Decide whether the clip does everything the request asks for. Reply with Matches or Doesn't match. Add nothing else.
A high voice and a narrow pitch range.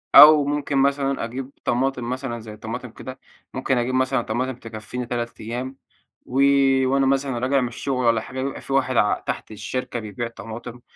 Doesn't match